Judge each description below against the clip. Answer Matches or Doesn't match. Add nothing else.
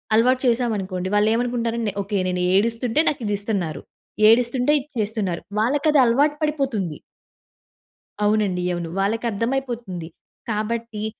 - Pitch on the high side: Matches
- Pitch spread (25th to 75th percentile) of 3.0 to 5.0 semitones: Matches